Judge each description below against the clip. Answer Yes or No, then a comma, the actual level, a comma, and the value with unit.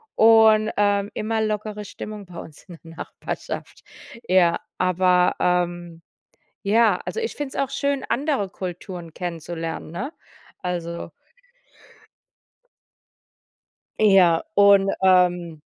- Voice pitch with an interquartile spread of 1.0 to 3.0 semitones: No, average, 3.7 semitones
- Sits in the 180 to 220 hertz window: Yes, medium, 185 Hz